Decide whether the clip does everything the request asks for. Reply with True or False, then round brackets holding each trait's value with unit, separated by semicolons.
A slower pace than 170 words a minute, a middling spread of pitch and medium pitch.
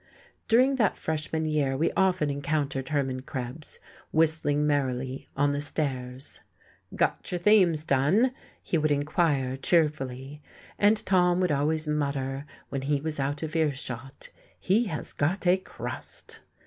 True (135 wpm; 3.4 semitones; 150 Hz)